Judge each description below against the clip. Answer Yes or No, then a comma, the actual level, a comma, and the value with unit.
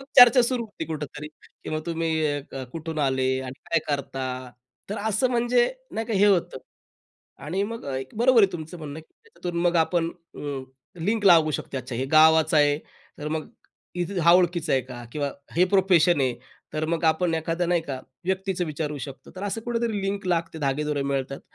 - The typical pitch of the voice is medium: Yes, medium, 160 Hz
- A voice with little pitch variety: No, average, 4.7 semitones